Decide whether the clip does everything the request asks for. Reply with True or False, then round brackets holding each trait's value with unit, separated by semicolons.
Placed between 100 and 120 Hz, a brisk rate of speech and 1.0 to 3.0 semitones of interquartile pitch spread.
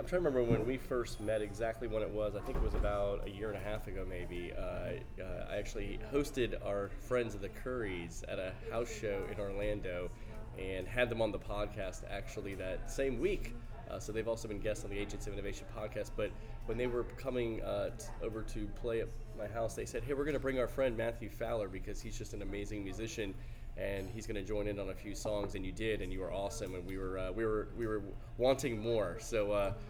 True (110 Hz; 245 wpm; 2.5 semitones)